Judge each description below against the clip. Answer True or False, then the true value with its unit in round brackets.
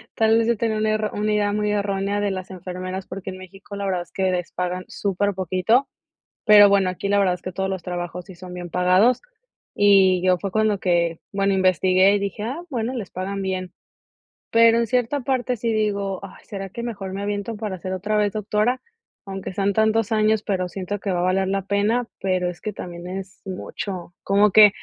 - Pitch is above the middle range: True (195 Hz)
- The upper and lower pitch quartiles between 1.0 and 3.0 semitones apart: True (2.4 semitones)